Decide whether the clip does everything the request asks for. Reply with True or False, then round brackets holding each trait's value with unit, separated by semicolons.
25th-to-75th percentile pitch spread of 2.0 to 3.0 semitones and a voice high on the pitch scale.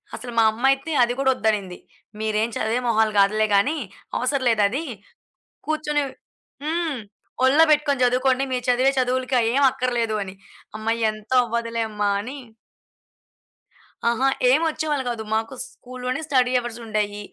False (3.6 semitones; 250 Hz)